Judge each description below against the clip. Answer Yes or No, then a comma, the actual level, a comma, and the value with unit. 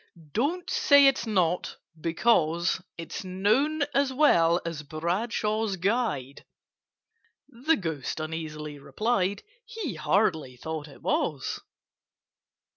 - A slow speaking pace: Yes, slow, 100 wpm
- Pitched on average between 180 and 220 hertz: Yes, medium, 185 Hz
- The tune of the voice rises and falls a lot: Yes, wide, 7.1 semitones